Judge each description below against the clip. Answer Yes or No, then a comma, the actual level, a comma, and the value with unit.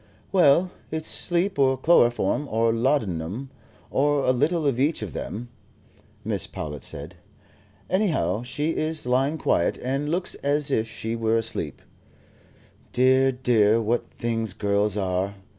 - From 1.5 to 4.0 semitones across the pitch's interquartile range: No, average, 5.2 semitones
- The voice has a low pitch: Yes, low, 125 Hz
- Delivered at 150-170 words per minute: No, slow, 135 wpm